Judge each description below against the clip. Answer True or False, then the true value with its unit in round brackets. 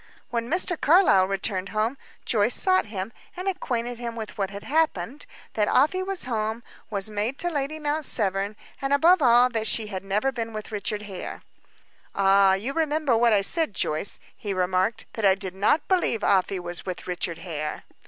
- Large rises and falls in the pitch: True (5.9 semitones)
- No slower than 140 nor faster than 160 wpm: False (185 wpm)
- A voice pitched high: True (220 Hz)